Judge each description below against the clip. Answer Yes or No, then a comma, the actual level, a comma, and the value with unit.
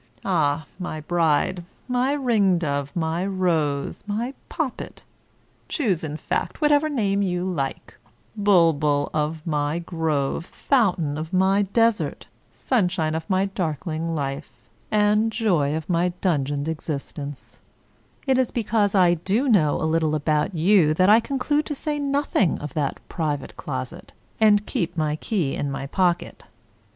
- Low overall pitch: No, medium, 175 Hz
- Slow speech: No, average, 145 wpm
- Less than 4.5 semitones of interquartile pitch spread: No, average, 5.3 semitones